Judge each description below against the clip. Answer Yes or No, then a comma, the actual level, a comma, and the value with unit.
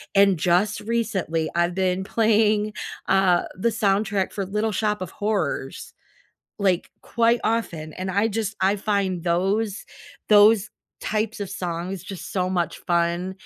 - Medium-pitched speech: No, high, 195 Hz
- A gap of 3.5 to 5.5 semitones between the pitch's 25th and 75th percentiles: No, average, 2.8 semitones